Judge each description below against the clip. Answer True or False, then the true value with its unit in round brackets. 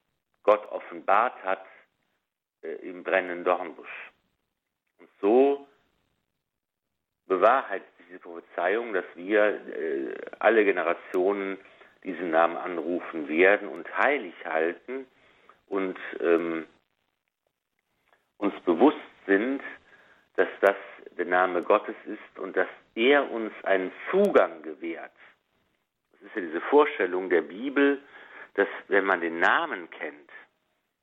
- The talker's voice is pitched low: True (130 Hz)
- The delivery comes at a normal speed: False (110 wpm)